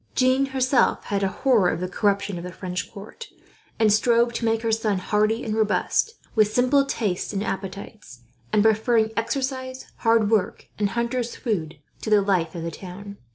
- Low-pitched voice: No, high, 215 Hz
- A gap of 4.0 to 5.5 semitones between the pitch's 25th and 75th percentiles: No, average, 3.3 semitones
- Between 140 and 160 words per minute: No, average, 180 wpm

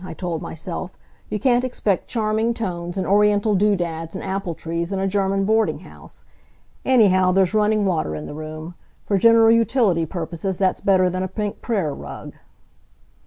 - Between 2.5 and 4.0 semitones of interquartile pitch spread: Yes, average, 3.6 semitones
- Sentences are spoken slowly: No, average, 170 wpm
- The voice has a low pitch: No, high, 195 Hz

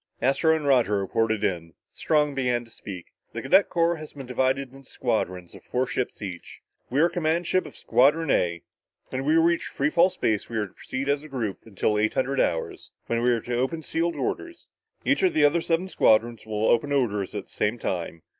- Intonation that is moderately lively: No, wide, 6.3 semitones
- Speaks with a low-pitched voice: Yes, low, 130 Hz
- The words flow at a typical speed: No, fast, 215 wpm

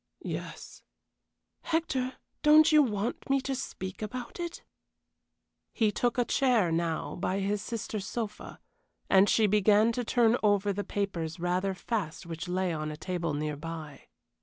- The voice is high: Yes, high, 205 Hz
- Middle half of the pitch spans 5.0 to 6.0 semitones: Yes, average, 5.3 semitones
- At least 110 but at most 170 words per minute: Yes, average, 150 wpm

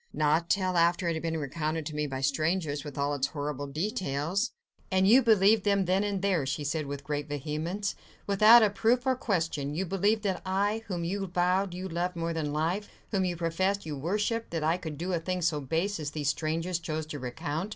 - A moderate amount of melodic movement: Yes, average, 4.4 semitones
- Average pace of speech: No, fast, 215 wpm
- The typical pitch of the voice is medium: Yes, medium, 170 Hz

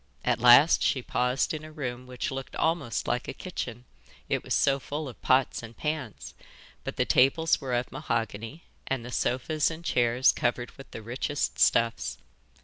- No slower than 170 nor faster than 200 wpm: Yes, average, 175 wpm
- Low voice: Yes, low, 130 Hz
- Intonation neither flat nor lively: Yes, average, 3.4 semitones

